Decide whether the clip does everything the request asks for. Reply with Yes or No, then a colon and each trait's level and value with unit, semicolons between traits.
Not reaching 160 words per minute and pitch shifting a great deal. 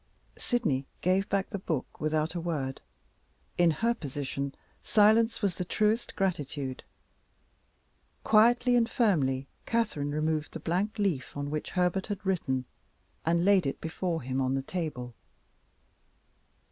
Yes: slow, 135 wpm; wide, 6.1 semitones